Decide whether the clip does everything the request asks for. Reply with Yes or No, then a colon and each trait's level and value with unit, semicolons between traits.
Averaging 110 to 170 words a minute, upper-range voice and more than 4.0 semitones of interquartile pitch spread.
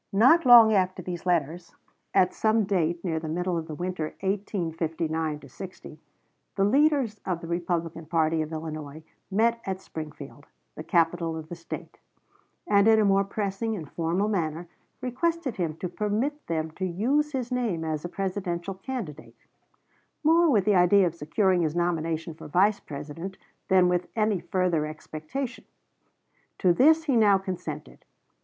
No: average, 155 wpm; medium, 180 Hz; average, 4.4 semitones